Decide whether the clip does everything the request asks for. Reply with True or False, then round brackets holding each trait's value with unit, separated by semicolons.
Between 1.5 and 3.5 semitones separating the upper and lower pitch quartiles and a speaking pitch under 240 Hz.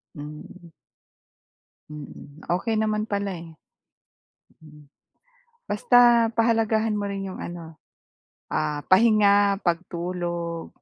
False (4.3 semitones; 190 Hz)